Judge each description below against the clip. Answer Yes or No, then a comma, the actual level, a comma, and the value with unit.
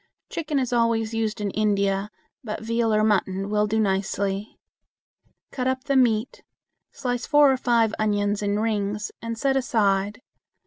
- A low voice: No, high, 215 Hz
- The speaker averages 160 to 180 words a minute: No, average, 150 wpm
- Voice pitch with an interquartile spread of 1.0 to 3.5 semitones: Yes, average, 2.8 semitones